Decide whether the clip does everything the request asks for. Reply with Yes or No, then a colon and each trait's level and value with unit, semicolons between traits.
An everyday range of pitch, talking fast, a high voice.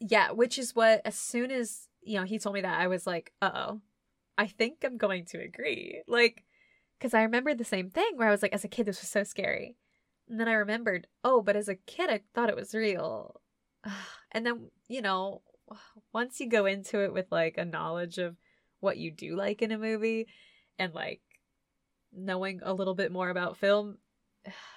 Yes: average, 3.2 semitones; fast, 210 wpm; high, 210 Hz